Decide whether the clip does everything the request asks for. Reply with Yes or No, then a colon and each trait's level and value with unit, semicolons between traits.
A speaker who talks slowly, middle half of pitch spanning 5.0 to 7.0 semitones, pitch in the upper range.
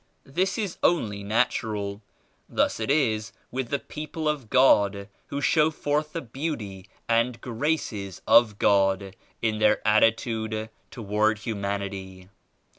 No: slow, 120 wpm; wide, 5.4 semitones; low, 110 Hz